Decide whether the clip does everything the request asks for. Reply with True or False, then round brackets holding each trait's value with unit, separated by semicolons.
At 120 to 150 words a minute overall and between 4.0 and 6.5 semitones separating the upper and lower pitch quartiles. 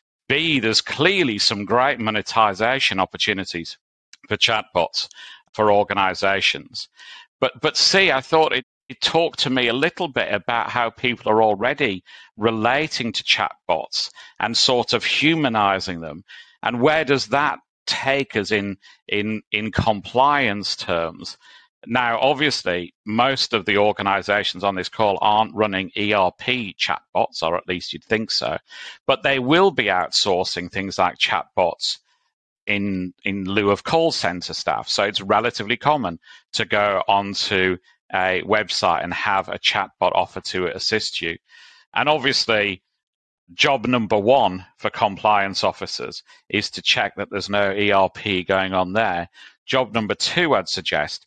True (145 wpm; 4.6 semitones)